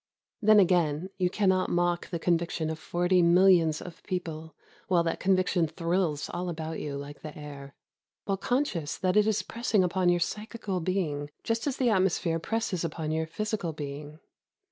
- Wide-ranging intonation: No, average, 3.2 semitones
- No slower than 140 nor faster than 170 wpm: No, average, 180 wpm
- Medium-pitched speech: Yes, medium, 175 Hz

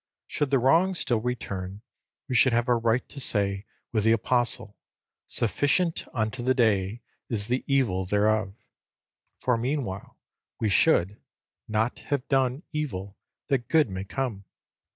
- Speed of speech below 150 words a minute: Yes, average, 140 wpm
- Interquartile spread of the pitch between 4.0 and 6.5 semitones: Yes, average, 4.3 semitones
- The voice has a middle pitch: No, low, 115 Hz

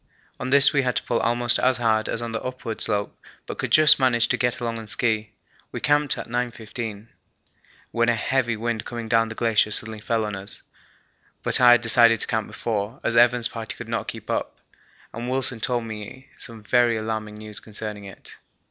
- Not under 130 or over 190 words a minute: No, average, 200 wpm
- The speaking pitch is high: No, low, 115 Hz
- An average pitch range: No, narrow, 1.9 semitones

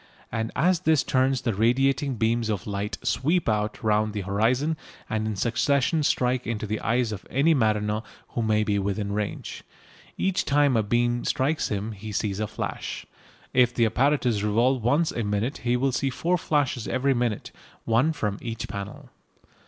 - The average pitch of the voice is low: Yes, low, 115 Hz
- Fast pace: No, average, 170 wpm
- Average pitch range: Yes, average, 4.1 semitones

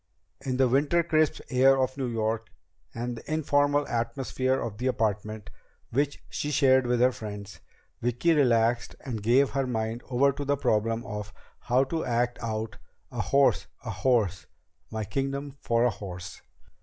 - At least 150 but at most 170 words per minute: Yes, average, 160 wpm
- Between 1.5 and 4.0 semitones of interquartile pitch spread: Yes, average, 3.5 semitones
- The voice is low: Yes, low, 125 Hz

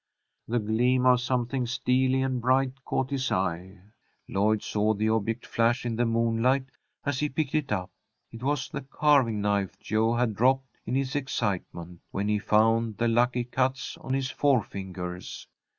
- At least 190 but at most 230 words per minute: No, average, 165 wpm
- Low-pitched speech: Yes, low, 120 Hz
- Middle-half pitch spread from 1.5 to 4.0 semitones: Yes, average, 3.5 semitones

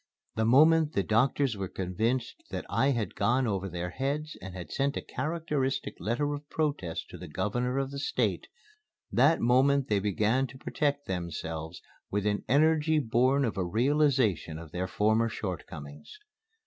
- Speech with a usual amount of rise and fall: No, wide, 6.6 semitones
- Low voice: Yes, low, 120 Hz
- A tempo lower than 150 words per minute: No, average, 160 wpm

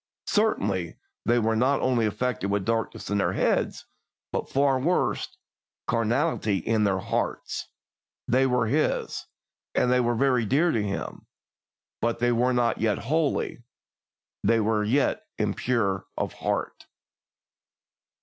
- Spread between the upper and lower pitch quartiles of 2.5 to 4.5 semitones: Yes, average, 3.3 semitones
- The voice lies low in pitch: Yes, low, 120 Hz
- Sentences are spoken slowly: Yes, slow, 130 wpm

